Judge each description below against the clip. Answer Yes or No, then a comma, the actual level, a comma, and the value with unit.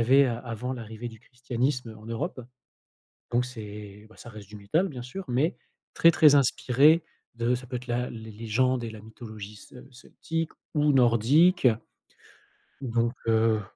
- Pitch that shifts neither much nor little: Yes, average, 3.0 semitones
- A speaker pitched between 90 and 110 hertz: No, low, 120 Hz